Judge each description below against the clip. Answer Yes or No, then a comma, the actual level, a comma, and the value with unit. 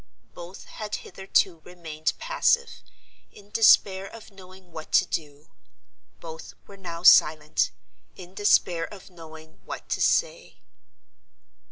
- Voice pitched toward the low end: No, medium, 180 Hz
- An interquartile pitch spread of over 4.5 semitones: No, average, 3.8 semitones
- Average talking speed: No, slow, 120 wpm